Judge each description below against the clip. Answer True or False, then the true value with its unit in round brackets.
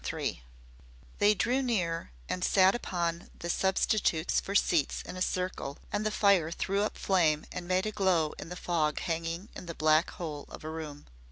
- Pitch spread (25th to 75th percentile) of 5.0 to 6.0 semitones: False (3.4 semitones)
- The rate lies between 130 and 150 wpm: False (185 wpm)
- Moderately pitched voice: True (180 Hz)